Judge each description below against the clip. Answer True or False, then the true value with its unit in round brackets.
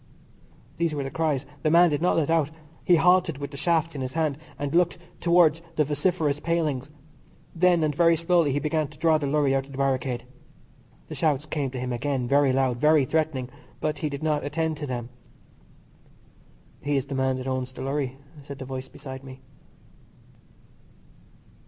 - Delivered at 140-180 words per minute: False (190 wpm)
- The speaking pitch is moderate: True (145 Hz)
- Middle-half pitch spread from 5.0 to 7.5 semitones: False (3.2 semitones)